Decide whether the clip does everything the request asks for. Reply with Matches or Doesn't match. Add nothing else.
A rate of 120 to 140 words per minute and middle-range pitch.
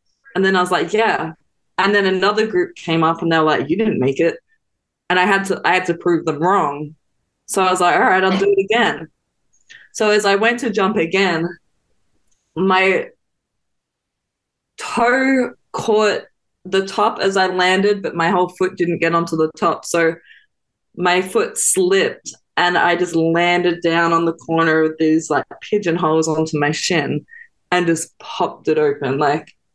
Doesn't match